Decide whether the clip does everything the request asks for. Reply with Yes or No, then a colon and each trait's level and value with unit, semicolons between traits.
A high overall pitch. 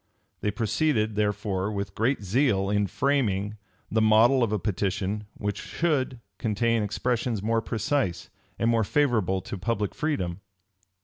No: low, 110 Hz